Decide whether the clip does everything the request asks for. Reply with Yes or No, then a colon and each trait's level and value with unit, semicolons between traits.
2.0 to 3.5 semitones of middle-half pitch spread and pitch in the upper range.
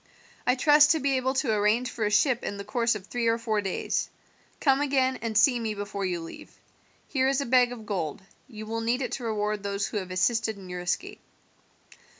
No: average, 4.1 semitones; high, 230 Hz